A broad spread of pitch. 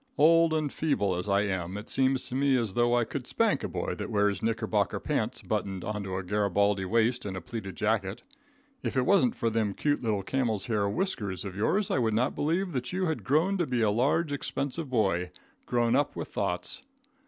Yes: wide, 5.7 semitones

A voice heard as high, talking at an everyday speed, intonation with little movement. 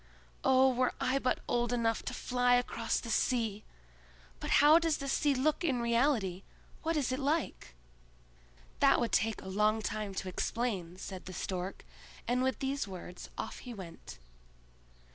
No: high, 240 Hz; average, 160 wpm; average, 4.9 semitones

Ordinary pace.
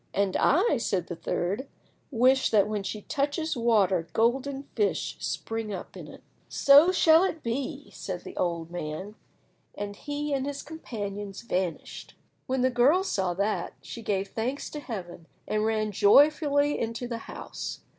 Yes: average, 155 wpm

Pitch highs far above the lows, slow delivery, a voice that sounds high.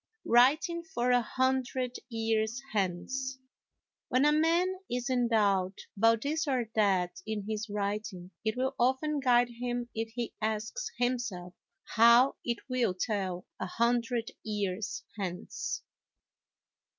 No: average, 3.5 semitones; slow, 125 wpm; high, 235 Hz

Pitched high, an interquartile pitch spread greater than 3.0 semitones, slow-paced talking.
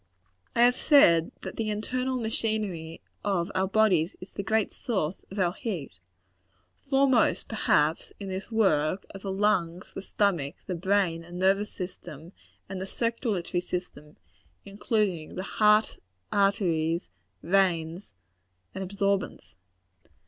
Yes: high, 195 Hz; average, 3.6 semitones; slow, 125 wpm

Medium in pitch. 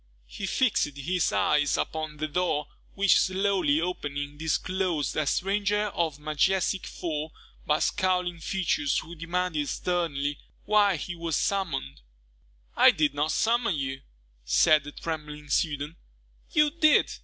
Yes: medium, 165 Hz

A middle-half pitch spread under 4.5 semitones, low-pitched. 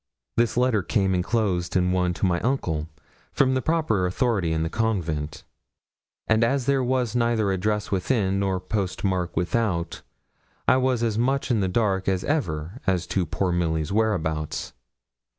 No: average, 4.8 semitones; low, 100 Hz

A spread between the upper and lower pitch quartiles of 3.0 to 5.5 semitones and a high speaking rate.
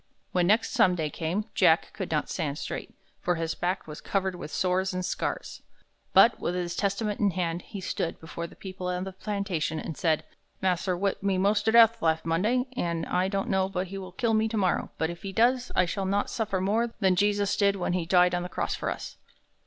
No: narrow, 2.4 semitones; fast, 225 wpm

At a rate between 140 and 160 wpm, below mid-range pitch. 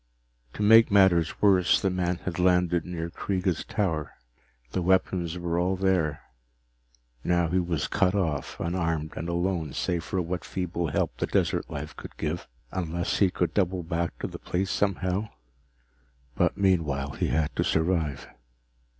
Yes: average, 155 wpm; very low, 90 Hz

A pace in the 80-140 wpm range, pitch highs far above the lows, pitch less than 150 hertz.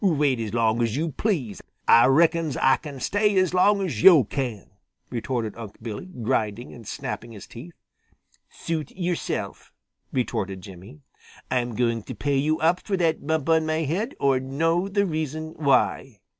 No: average, 165 wpm; wide, 5.9 semitones; medium, 140 Hz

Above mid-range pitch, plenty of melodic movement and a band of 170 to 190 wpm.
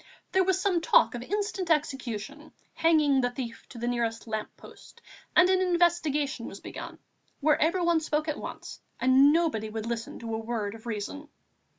Yes: very high, 285 Hz; wide, 6.3 semitones; average, 175 wpm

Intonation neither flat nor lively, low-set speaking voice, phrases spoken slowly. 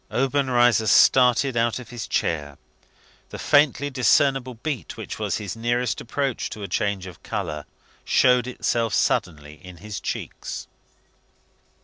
Yes: average, 4.6 semitones; low, 120 Hz; slow, 130 wpm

